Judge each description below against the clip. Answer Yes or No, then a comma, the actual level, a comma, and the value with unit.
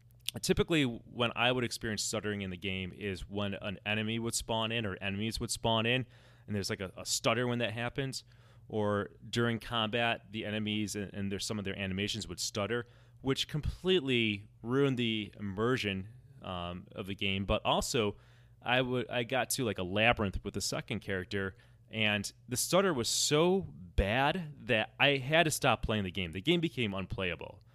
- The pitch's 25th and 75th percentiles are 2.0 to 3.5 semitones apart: Yes, average, 3.2 semitones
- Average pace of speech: Yes, average, 185 wpm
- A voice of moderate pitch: No, low, 115 Hz